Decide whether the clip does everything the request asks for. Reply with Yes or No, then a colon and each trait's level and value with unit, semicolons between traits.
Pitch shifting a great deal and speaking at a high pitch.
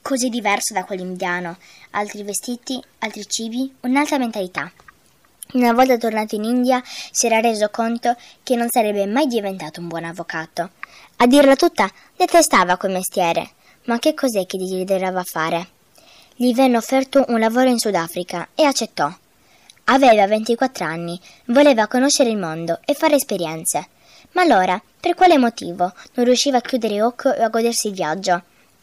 Yes: wide, 5.7 semitones; high, 225 Hz